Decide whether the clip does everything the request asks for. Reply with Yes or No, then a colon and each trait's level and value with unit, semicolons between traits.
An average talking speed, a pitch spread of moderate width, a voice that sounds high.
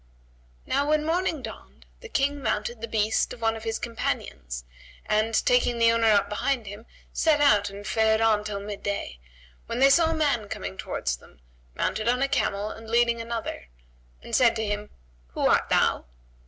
Yes: average, 185 wpm; average, 3.2 semitones; high, 225 Hz